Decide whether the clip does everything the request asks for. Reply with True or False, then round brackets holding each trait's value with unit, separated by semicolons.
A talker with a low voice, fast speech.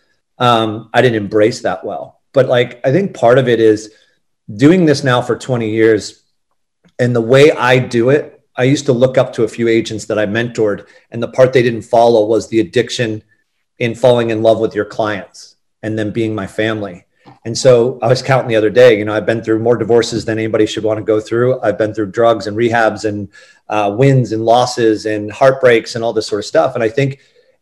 True (115 Hz; 220 wpm)